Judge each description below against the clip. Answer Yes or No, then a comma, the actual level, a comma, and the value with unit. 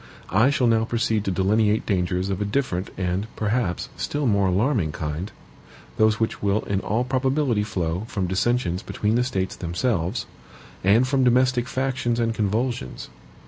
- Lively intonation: No, average, 4.5 semitones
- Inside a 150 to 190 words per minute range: Yes, average, 155 wpm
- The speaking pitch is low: Yes, low, 110 Hz